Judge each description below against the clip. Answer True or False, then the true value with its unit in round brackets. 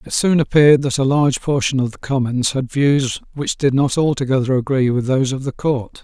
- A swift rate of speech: True (220 wpm)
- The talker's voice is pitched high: False (135 Hz)